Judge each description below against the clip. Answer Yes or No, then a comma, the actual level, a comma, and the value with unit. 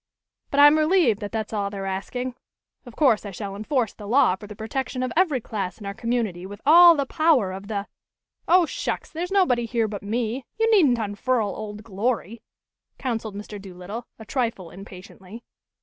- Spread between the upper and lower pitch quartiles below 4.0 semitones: No, average, 4.7 semitones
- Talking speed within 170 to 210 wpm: Yes, average, 185 wpm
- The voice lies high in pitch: Yes, high, 225 Hz